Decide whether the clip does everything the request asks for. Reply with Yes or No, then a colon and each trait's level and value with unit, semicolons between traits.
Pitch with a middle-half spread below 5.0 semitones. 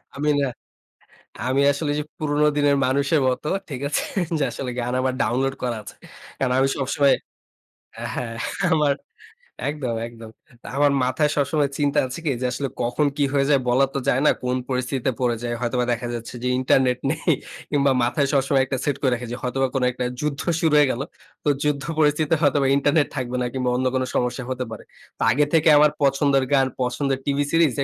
Yes: narrow, 2.5 semitones